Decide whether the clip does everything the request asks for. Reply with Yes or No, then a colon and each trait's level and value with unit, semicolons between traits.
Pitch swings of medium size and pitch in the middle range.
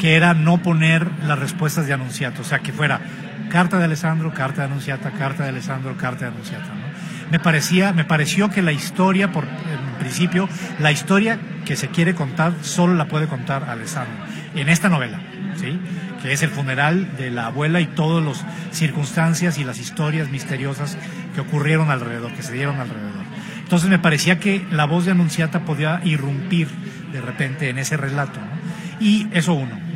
Yes: average, 3.3 semitones; medium, 160 Hz